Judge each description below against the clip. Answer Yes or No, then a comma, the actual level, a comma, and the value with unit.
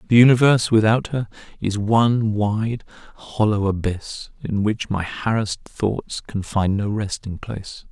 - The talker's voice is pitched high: No, low, 105 Hz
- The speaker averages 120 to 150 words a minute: Yes, average, 145 wpm